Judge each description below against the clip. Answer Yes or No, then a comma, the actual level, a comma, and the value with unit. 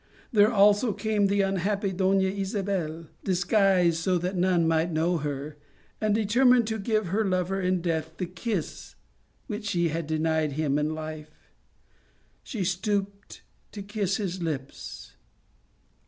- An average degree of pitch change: Yes, average, 3.7 semitones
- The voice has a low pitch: No, medium, 185 Hz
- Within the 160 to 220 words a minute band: No, average, 140 wpm